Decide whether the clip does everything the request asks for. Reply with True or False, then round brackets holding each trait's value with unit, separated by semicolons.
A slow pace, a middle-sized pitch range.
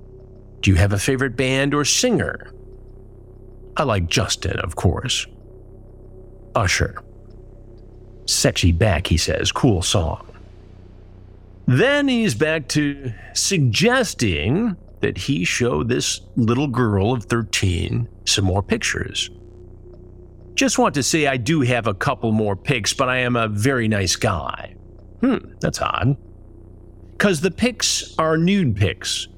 False (130 wpm; 6.1 semitones)